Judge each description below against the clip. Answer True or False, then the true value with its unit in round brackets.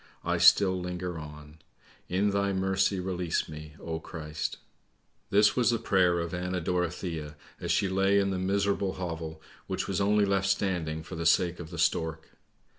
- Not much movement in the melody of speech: False (3.1 semitones)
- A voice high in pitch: False (90 Hz)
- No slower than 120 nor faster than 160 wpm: False (180 wpm)